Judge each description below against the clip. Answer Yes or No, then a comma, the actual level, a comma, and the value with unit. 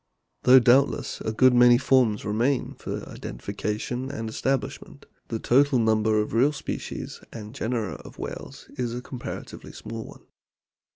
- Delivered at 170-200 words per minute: No, average, 140 wpm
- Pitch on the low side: Yes, low, 120 Hz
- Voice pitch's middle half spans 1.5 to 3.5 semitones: Yes, average, 2.9 semitones